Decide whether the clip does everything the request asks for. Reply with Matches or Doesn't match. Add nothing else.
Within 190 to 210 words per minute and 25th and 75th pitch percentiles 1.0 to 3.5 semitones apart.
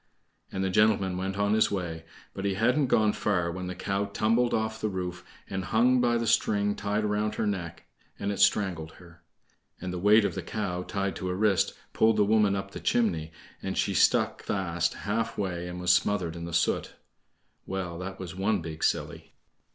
Matches